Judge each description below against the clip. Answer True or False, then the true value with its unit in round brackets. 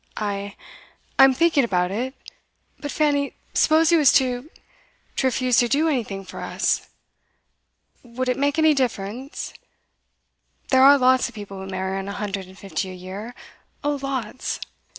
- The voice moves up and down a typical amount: False (5.9 semitones)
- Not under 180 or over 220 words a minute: False (155 wpm)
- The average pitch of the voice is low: False (250 Hz)